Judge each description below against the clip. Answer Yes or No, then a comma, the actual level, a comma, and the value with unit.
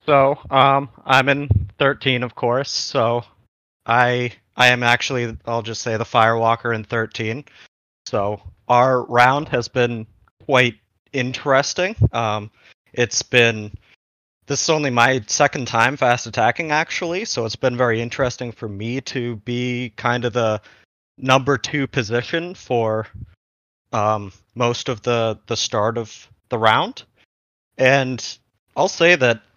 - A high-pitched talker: No, low, 120 Hz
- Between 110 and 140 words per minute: Yes, slow, 135 wpm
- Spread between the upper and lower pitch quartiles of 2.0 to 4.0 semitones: Yes, average, 2.9 semitones